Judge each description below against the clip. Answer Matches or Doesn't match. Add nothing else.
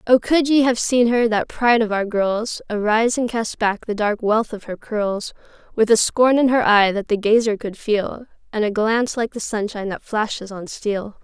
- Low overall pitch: Doesn't match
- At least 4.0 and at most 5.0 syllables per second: Matches